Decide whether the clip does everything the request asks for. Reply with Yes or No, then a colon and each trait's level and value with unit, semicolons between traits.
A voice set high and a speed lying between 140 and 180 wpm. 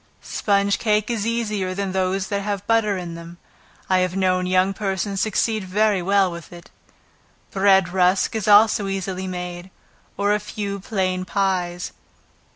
Yes: high, 195 Hz; average, 155 wpm